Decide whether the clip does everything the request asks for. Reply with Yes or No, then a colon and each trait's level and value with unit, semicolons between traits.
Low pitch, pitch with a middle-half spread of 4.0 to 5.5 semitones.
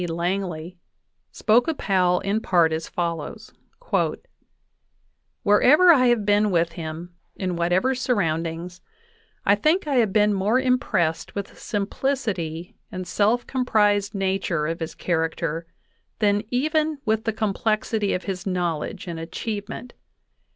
No: high, 195 Hz; average, 4.5 semitones